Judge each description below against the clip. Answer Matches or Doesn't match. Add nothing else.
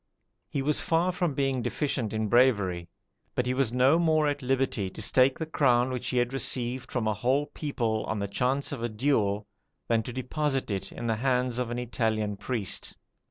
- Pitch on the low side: Matches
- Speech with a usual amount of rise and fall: Matches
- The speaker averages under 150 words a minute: Doesn't match